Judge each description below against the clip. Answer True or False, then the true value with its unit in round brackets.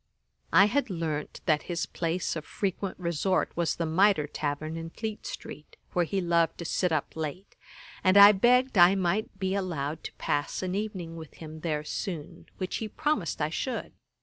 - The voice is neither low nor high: True (175 Hz)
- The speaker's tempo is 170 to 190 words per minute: True (180 wpm)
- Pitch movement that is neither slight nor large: True (3.6 semitones)